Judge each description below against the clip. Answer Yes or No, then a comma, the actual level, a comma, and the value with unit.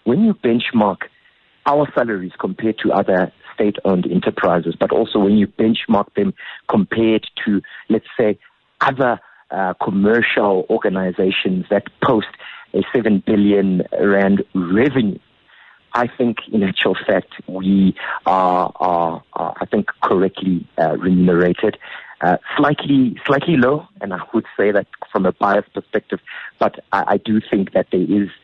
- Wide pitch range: No, average, 3.4 semitones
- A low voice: Yes, low, 100 Hz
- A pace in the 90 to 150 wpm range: Yes, average, 140 wpm